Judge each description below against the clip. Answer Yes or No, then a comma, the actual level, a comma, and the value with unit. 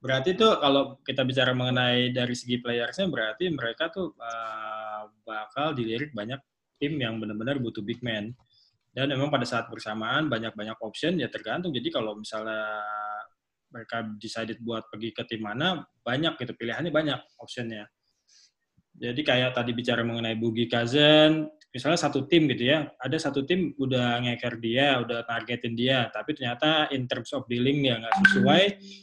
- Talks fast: Yes, fast, 155 wpm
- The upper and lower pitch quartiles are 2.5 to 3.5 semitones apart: No, average, 3.9 semitones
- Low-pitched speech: Yes, low, 120 Hz